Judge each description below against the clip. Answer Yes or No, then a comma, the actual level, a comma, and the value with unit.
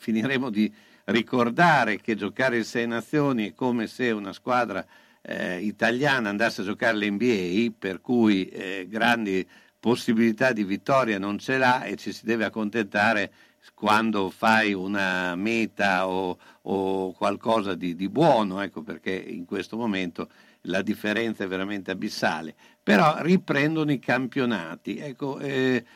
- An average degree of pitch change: Yes, average, 3.8 semitones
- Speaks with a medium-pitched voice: No, low, 110 Hz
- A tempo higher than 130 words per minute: Yes, average, 140 wpm